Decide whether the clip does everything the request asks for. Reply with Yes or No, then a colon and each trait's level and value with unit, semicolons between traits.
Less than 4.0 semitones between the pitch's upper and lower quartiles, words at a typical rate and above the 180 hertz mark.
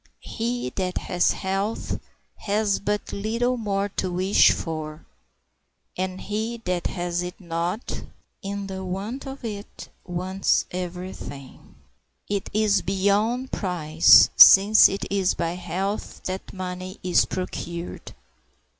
No: narrow, 2.5 semitones; slow, 120 wpm; high, 190 Hz